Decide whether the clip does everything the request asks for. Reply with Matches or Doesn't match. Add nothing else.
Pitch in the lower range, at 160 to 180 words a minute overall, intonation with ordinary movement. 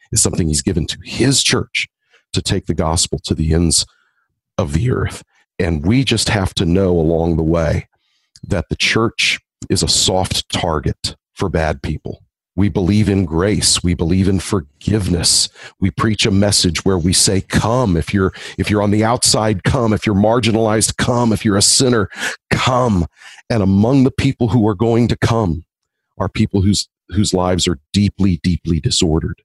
Matches